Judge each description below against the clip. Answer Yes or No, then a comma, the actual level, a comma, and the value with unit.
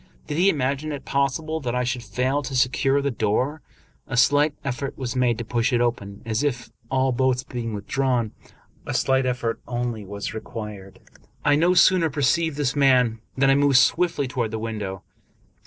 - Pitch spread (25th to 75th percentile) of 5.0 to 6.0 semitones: No, average, 3.3 semitones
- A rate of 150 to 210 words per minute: Yes, average, 175 wpm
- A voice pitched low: Yes, low, 130 Hz